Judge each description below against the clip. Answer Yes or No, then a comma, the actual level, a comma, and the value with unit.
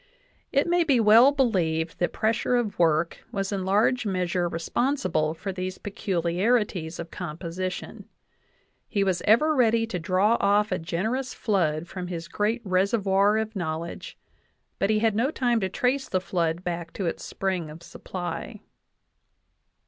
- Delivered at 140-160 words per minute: Yes, average, 155 wpm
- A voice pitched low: No, high, 190 Hz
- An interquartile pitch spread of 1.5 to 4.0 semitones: No, average, 4.6 semitones